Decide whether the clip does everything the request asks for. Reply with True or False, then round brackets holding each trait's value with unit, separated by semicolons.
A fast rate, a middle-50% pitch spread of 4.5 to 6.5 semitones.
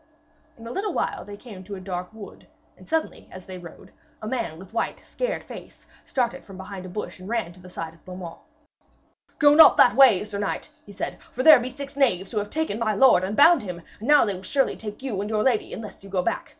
True (245 wpm; 5.4 semitones)